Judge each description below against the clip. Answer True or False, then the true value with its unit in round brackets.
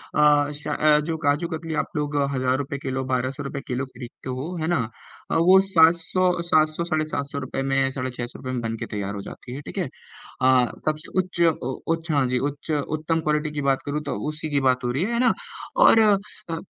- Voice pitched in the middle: True (145 Hz)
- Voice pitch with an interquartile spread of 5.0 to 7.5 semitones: False (3.5 semitones)